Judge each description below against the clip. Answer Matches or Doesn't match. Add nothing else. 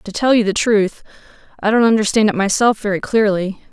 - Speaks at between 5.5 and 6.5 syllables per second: Matches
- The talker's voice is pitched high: Matches